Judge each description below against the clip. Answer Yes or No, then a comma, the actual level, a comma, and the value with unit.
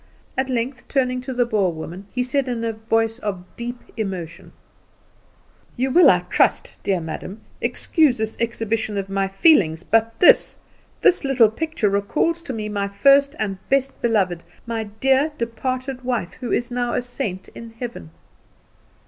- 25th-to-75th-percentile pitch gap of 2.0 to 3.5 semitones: No, average, 4.2 semitones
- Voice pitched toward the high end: Yes, high, 230 Hz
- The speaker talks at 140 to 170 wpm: Yes, average, 160 wpm